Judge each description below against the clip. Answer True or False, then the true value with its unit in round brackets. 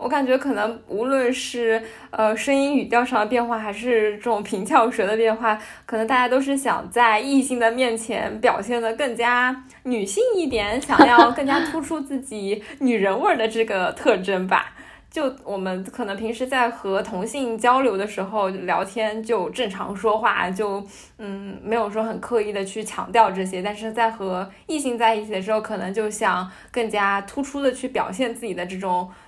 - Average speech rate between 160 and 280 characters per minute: True (275 characters per minute)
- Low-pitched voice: False (225 Hz)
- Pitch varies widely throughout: False (3.2 semitones)